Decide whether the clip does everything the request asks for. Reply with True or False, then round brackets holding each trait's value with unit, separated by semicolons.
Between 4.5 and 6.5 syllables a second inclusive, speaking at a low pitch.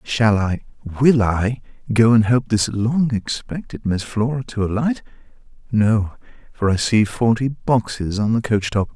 False (4.1 syllables/s; 115 Hz)